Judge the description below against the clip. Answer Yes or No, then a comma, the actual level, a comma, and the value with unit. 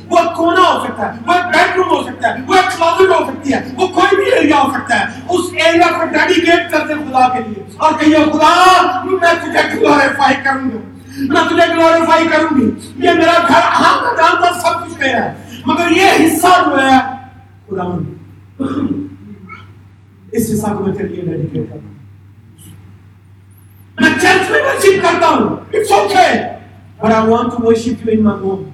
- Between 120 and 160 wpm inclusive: No, fast, 190 wpm